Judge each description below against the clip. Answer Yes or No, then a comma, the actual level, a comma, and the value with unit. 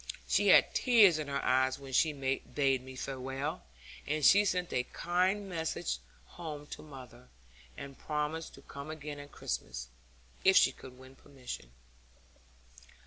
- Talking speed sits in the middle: Yes, average, 145 wpm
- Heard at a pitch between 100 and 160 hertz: Yes, medium, 140 Hz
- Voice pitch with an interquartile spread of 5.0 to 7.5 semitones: No, average, 3.5 semitones